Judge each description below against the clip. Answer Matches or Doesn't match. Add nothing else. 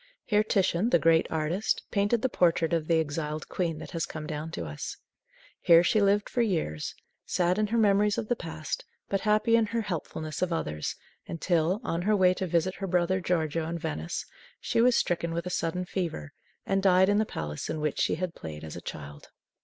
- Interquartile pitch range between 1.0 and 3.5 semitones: Doesn't match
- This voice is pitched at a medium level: Matches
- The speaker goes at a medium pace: Doesn't match